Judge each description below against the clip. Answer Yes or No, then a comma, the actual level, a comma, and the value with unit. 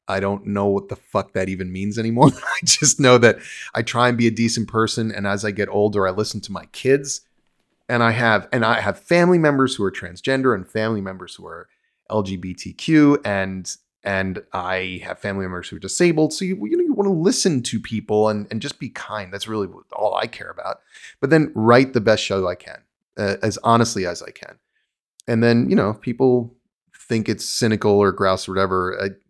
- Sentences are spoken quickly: Yes, fast, 215 wpm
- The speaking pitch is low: Yes, low, 110 Hz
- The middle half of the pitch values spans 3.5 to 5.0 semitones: Yes, average, 4.0 semitones